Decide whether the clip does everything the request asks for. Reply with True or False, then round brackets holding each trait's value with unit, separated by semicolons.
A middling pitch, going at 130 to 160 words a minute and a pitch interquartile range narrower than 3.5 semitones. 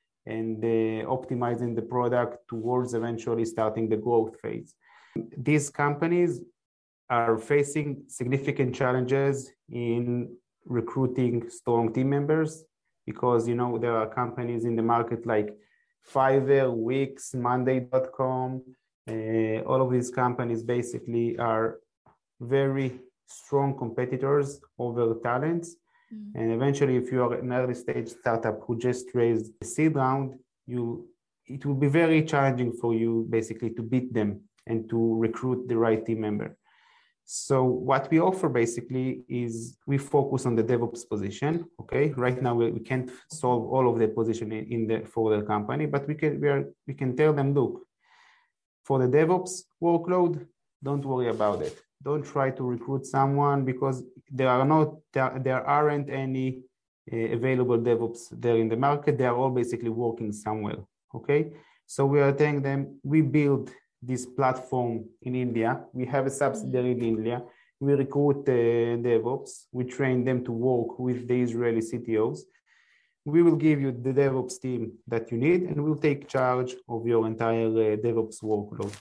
False (125 Hz; 155 wpm; 3.1 semitones)